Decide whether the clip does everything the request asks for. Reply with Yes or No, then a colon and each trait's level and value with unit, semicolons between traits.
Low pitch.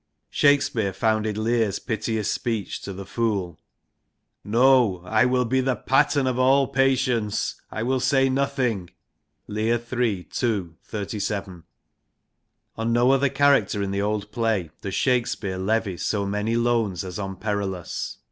Yes: low, 110 Hz